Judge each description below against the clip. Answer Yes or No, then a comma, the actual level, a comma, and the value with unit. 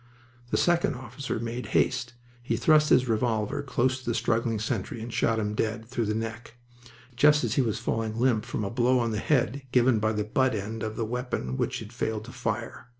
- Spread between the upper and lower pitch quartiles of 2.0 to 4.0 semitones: Yes, narrow, 2.4 semitones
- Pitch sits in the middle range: No, low, 115 Hz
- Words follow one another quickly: Yes, fast, 210 wpm